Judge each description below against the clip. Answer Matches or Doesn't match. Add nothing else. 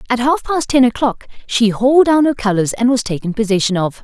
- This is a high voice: Matches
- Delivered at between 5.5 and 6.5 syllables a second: Matches